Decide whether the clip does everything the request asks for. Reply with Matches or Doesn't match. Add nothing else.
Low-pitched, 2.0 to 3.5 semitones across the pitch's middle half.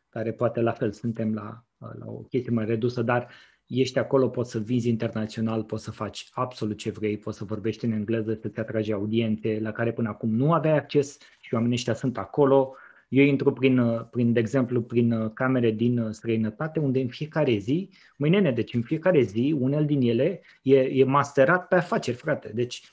Matches